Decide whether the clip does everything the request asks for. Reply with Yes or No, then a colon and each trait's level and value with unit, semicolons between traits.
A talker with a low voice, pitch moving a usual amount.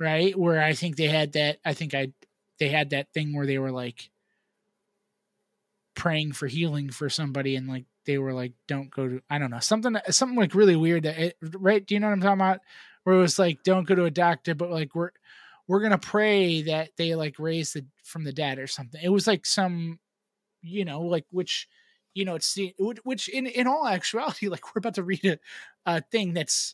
No: medium, 170 Hz; average, 4.9 semitones